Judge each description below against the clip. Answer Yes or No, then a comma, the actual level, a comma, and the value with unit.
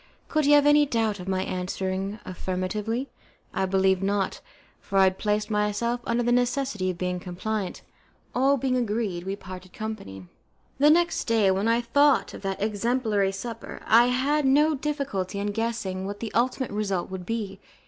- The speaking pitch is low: No, high, 210 Hz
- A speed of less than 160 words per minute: No, average, 170 wpm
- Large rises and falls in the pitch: No, average, 4.4 semitones